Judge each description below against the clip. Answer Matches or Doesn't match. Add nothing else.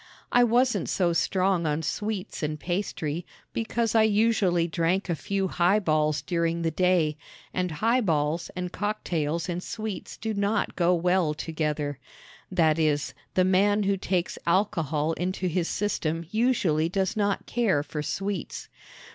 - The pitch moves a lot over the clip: Doesn't match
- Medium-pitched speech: Matches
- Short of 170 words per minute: Matches